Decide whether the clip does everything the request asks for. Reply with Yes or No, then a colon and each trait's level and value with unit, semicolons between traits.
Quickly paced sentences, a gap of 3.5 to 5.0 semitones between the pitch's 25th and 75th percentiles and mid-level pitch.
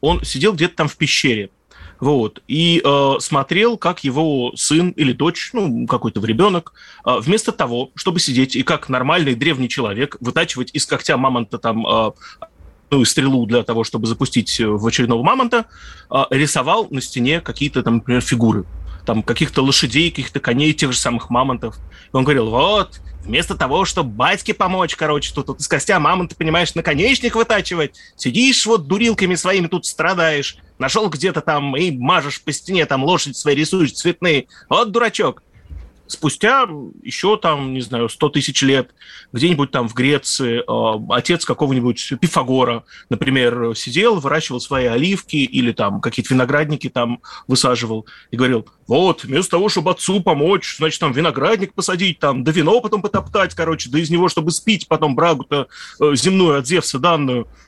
No: fast, 165 wpm; wide, 5.6 semitones; medium, 145 Hz